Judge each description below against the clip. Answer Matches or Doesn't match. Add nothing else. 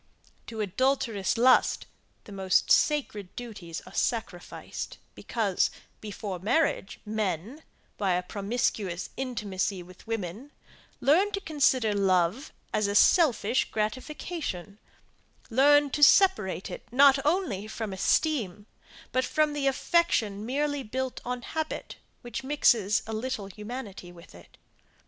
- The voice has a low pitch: Doesn't match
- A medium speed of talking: Doesn't match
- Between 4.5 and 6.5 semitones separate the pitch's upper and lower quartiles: Matches